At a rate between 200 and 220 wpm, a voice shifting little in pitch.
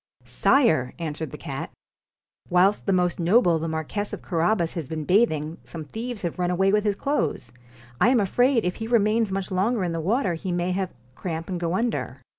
No: fast, 205 wpm; average, 4.3 semitones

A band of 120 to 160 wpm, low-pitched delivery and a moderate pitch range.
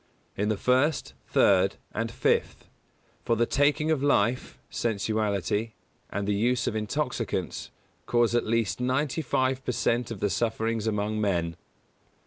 Yes: average, 140 wpm; low, 115 Hz; average, 3.3 semitones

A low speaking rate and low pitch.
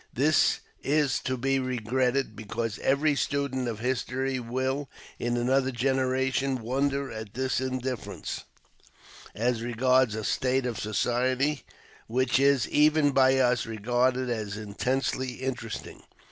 Yes: slow, 120 wpm; low, 130 Hz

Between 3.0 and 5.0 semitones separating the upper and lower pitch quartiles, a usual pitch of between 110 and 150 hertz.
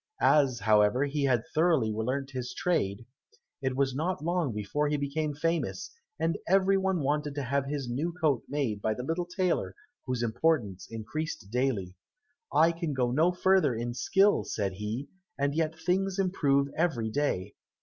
No: wide, 5.5 semitones; medium, 140 Hz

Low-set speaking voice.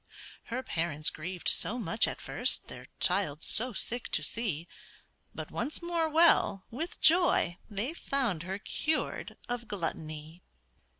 No: high, 210 Hz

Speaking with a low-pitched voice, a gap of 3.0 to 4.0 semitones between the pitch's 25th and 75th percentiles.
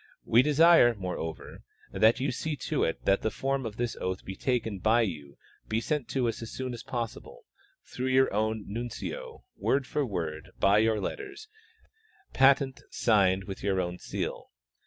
No: low, 115 Hz; average, 5.1 semitones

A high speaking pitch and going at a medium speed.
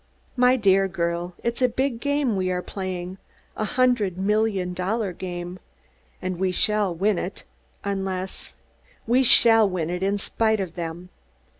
Yes: high, 195 Hz; average, 150 wpm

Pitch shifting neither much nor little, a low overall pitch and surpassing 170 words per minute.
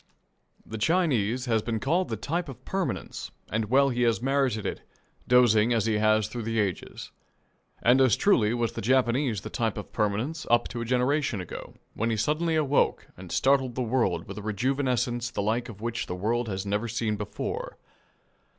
Yes: average, 3.4 semitones; low, 120 Hz; average, 185 wpm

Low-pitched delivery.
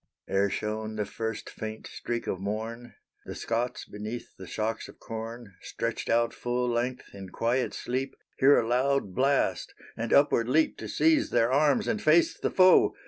Yes: low, 120 Hz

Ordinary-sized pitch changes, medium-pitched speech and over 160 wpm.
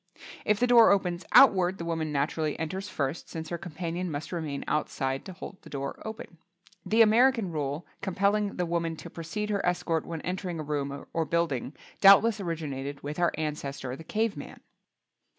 Yes: average, 4.5 semitones; medium, 170 Hz; average, 175 wpm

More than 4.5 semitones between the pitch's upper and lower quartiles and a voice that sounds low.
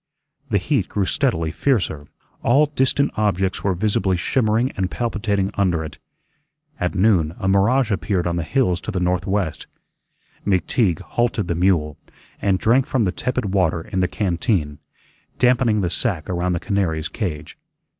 No: average, 4.0 semitones; very low, 95 Hz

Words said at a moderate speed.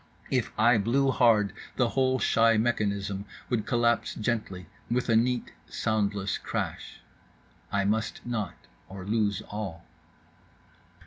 No: slow, 120 wpm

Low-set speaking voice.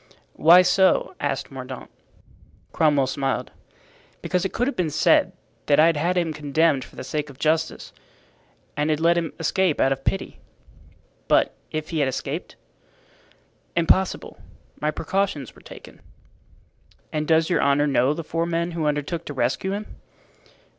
No: medium, 155 Hz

